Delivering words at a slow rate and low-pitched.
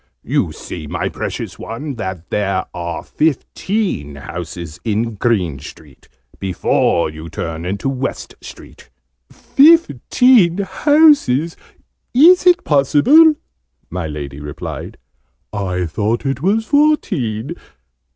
Yes: slow, 105 wpm; low, 115 Hz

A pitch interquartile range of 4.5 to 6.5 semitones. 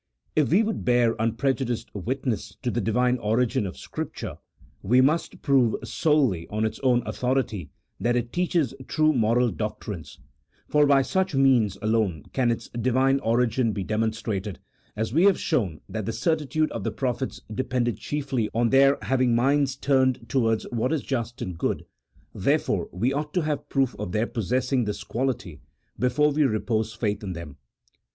No: average, 3.6 semitones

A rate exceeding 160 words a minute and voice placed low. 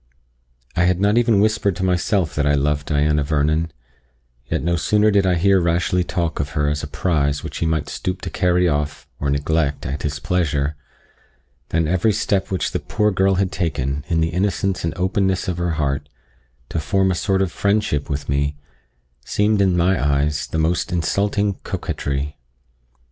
Yes: average, 180 wpm; very low, 85 Hz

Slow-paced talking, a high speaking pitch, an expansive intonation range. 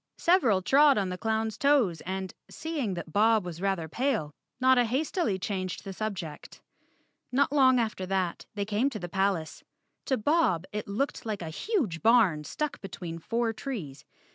No: average, 165 wpm; high, 210 Hz; wide, 6.0 semitones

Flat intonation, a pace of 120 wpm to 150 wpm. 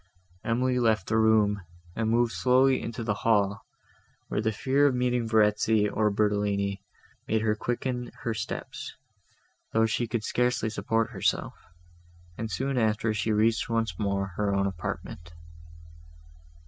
Yes: narrow, 2.3 semitones; average, 140 wpm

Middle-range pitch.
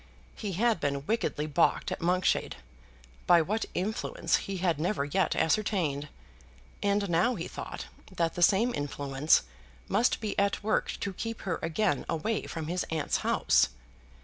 Yes: medium, 180 Hz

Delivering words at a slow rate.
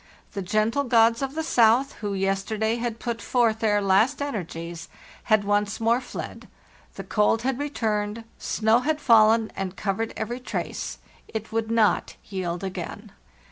No: average, 150 wpm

